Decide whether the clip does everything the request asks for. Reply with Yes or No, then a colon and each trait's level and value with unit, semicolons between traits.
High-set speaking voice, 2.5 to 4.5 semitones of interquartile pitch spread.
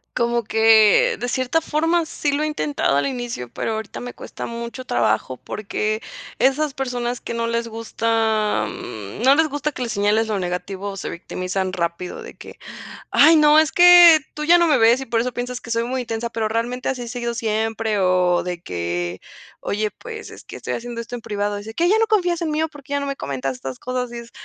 No: high, 235 Hz; average, 5.2 semitones